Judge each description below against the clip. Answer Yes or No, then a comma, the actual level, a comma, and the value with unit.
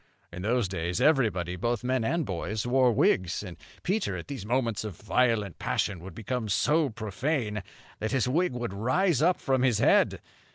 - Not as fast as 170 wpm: No, average, 175 wpm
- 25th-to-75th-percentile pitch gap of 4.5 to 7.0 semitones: Yes, average, 4.9 semitones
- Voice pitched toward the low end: Yes, low, 115 Hz